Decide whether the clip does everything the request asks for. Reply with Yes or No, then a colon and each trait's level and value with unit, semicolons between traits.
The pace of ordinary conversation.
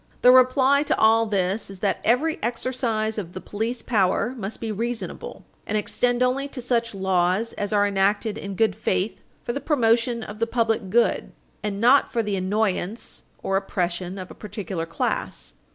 Yes: average, 175 wpm